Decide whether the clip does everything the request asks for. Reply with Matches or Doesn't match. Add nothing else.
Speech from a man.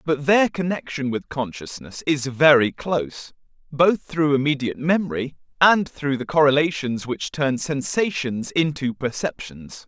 Matches